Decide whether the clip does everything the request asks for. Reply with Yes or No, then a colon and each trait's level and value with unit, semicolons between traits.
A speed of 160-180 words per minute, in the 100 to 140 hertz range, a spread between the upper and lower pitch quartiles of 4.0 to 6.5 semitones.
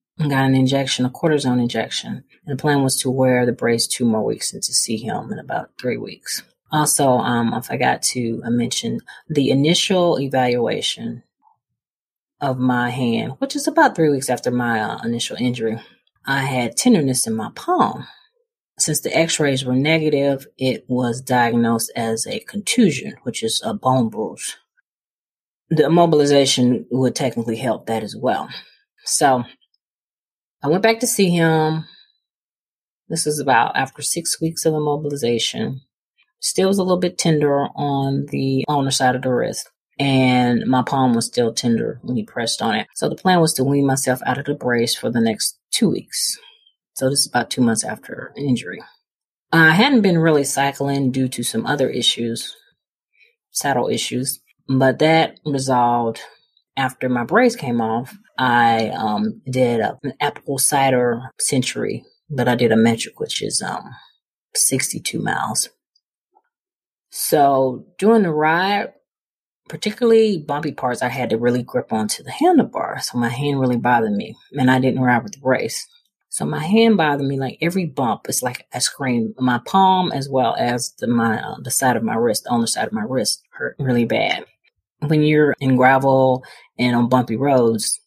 Yes: average, 170 wpm; low, 135 Hz; average, 4.4 semitones